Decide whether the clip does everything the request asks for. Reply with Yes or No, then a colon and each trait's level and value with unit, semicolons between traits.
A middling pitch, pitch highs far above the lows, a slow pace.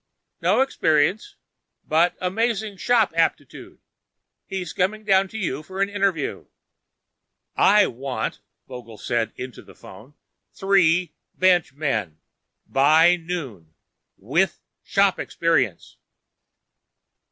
Yes: medium, 170 Hz; wide, 6.3 semitones; slow, 100 wpm